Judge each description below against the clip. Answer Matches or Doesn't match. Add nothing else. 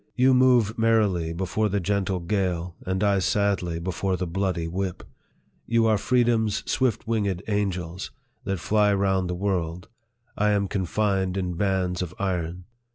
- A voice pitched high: Doesn't match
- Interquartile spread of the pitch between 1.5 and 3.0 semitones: Matches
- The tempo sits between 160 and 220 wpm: Doesn't match